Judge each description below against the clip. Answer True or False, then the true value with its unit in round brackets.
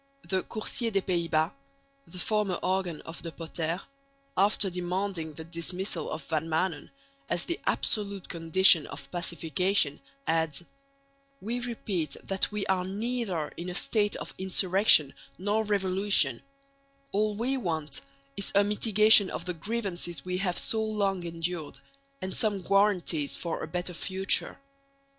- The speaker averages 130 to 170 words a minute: True (140 wpm)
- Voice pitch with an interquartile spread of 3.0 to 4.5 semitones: True (3.4 semitones)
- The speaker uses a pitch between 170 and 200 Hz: True (185 Hz)